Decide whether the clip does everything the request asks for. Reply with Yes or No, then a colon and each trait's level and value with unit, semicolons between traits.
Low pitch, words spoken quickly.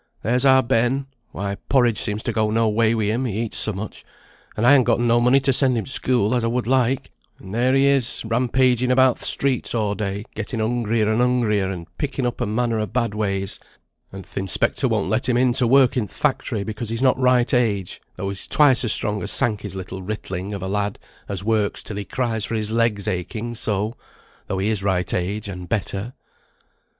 Yes: low, 115 Hz; fast, 220 wpm